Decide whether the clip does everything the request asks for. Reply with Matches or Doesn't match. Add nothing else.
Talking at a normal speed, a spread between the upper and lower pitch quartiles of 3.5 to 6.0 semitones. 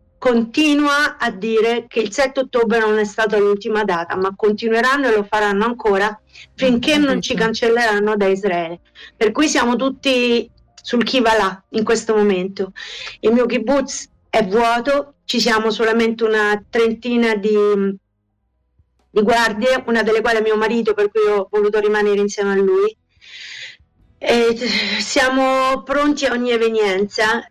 Doesn't match